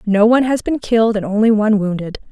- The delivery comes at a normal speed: No, fast, 235 wpm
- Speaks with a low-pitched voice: No, high, 215 Hz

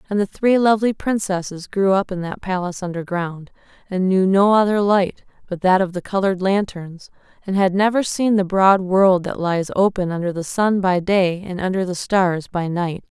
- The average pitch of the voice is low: No, high, 190 Hz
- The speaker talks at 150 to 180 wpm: No, average, 195 wpm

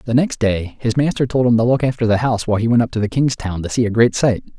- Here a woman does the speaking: No, male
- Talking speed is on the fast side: Yes, fast, 325 wpm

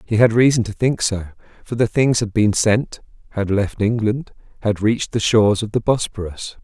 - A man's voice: Yes, male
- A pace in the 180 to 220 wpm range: Yes, average, 200 wpm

